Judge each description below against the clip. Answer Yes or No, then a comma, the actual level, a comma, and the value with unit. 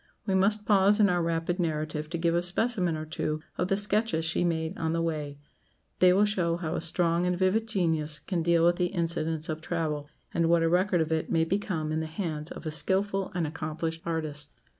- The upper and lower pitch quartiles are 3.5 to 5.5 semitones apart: No, narrow, 2.6 semitones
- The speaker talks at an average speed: No, fast, 220 wpm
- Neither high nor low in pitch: Yes, medium, 170 Hz